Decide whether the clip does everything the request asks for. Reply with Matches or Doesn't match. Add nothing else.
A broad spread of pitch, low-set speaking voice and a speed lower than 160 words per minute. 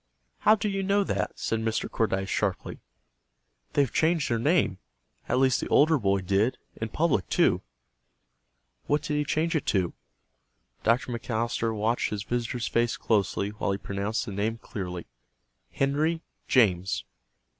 Matches